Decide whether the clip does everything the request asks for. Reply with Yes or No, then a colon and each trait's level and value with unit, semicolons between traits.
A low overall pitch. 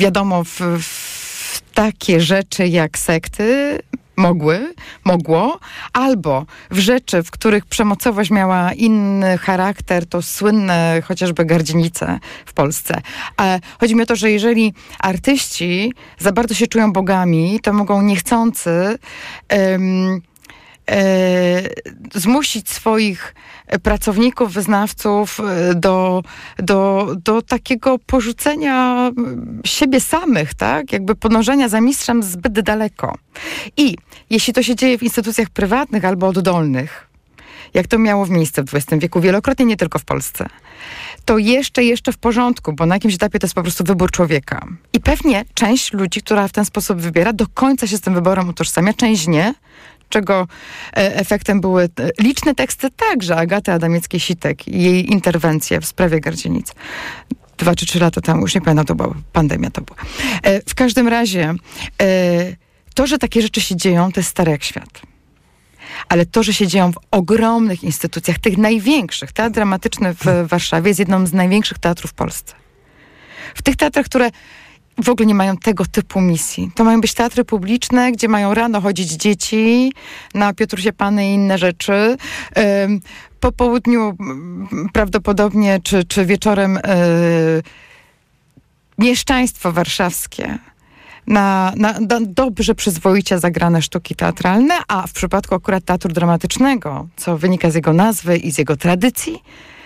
No: high, 200 Hz